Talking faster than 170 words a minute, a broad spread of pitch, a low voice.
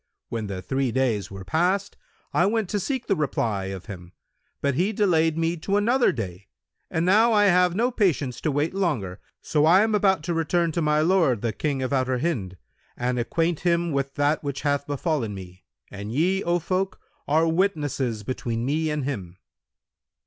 No: average, 185 wpm; wide, 6.6 semitones; medium, 150 Hz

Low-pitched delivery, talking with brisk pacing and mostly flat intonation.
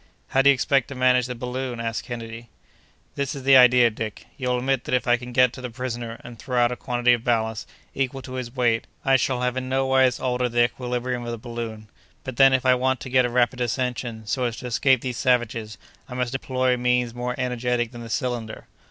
Yes: low, 125 Hz; fast, 230 wpm; narrow, 1.4 semitones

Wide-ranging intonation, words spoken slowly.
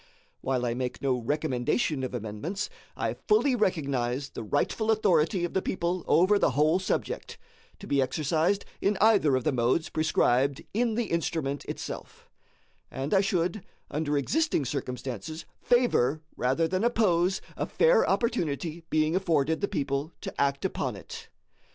No: wide, 6.0 semitones; average, 150 wpm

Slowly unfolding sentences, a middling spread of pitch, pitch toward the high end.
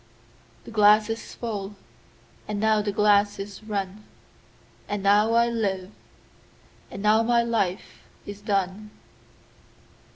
No: slow, 110 wpm; narrow, 1.8 semitones; high, 205 Hz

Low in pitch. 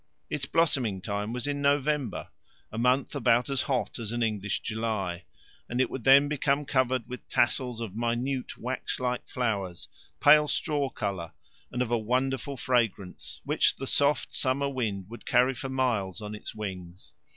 Yes: low, 125 Hz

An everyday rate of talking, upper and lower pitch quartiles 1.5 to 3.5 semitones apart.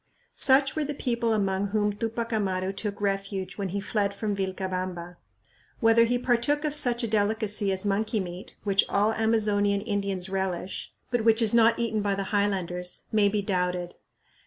Yes: average, 170 wpm; average, 2.7 semitones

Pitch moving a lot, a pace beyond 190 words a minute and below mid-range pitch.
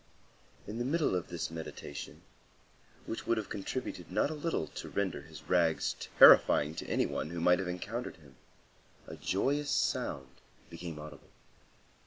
No: wide, 6.5 semitones; average, 155 wpm; very low, 90 Hz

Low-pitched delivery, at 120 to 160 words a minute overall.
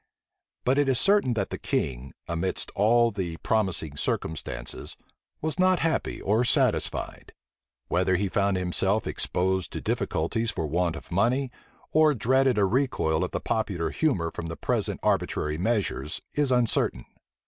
Yes: low, 100 Hz; average, 150 wpm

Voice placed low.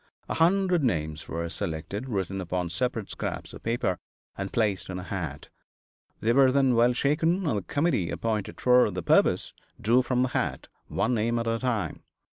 Yes: low, 115 Hz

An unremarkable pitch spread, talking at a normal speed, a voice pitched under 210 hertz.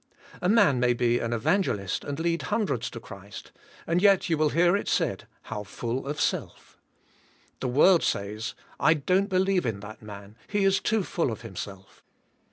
No: wide, 8.9 semitones; average, 180 wpm; low, 135 Hz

